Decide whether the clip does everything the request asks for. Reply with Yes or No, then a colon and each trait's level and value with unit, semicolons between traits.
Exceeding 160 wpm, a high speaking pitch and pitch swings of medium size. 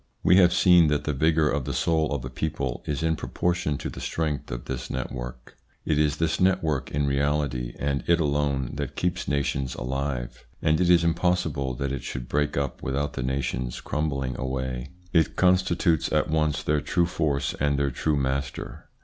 No: average, 190 wpm; very low, 70 Hz; average, 3.1 semitones